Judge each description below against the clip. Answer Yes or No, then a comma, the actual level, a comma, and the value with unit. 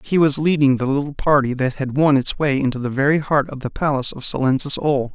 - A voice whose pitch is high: No, medium, 140 Hz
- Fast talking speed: Yes, fast, 245 wpm